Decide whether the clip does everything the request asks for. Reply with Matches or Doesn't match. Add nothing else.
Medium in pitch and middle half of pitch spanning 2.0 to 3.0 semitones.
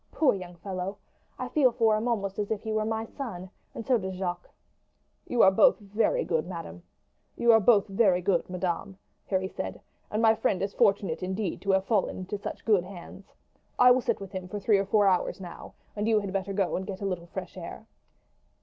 Doesn't match